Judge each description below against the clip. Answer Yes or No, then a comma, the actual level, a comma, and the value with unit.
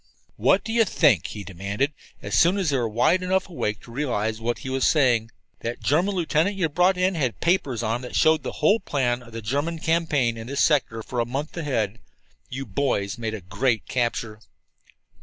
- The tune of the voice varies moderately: No, wide, 6.3 semitones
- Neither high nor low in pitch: No, low, 130 Hz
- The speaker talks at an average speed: No, fast, 210 wpm